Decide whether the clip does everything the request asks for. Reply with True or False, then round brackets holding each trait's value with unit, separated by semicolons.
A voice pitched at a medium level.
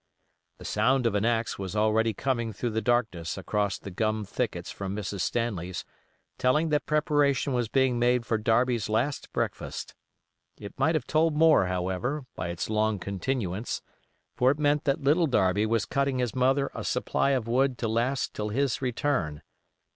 False (120 Hz)